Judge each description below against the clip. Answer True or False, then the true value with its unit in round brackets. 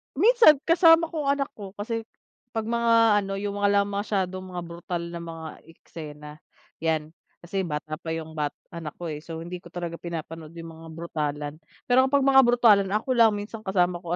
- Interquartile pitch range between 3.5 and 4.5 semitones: False (5.6 semitones)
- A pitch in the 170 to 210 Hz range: True (185 Hz)